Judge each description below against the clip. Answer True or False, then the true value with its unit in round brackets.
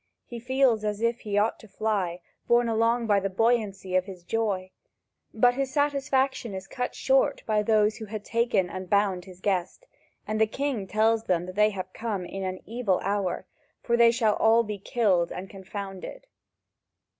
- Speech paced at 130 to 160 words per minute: False (180 wpm)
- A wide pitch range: False (3.4 semitones)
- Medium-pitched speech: False (215 Hz)